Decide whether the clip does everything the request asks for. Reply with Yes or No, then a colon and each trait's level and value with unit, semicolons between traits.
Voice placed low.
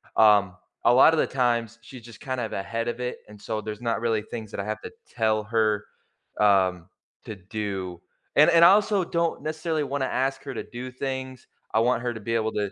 Yes: low, 115 Hz